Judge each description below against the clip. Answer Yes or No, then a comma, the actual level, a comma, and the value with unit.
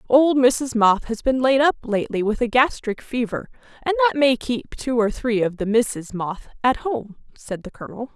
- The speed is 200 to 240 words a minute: Yes, fast, 205 wpm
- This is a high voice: Yes, high, 240 Hz